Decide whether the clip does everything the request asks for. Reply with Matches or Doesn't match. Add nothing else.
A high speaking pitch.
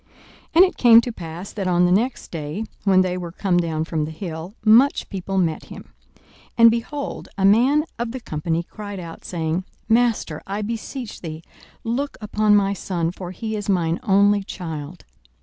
Matches